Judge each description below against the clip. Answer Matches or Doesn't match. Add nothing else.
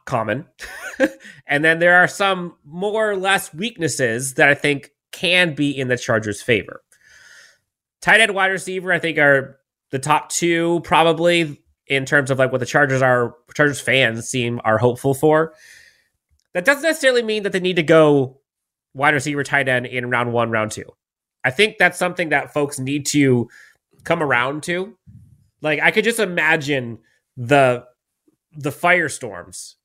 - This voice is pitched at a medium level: Matches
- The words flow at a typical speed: Matches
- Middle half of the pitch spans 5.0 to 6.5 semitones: Matches